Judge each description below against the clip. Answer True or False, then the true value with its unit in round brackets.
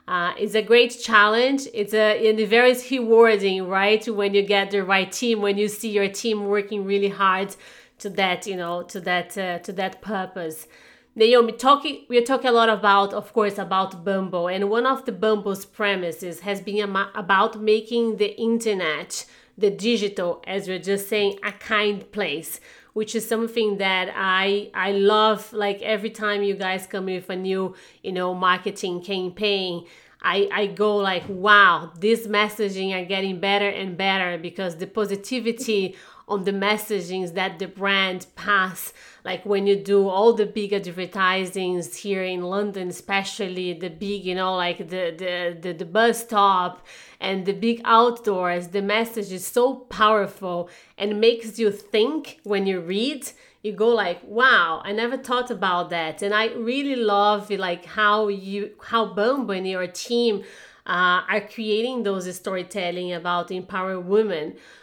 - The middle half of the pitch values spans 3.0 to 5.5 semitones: False (2.5 semitones)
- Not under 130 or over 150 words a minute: False (170 wpm)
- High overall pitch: True (200 Hz)